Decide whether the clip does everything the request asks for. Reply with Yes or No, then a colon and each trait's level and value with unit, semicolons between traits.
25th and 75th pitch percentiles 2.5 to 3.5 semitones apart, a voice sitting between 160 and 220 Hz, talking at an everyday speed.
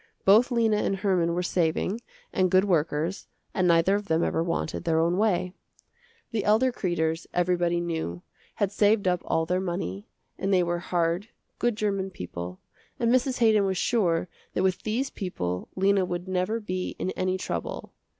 Yes: average, 3.2 semitones; medium, 185 Hz; average, 170 wpm